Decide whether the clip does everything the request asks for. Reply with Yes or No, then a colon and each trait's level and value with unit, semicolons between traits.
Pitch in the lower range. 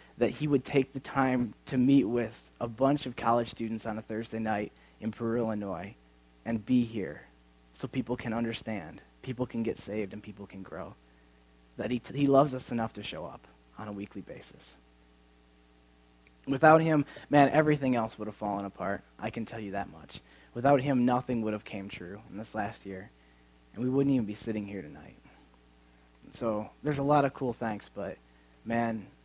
Yes: low, 110 Hz